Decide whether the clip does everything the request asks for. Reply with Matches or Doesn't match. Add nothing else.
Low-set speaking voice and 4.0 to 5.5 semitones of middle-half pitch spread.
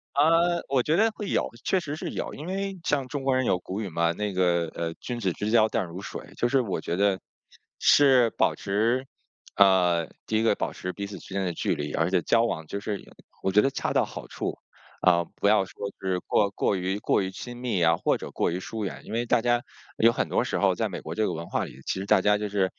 Matches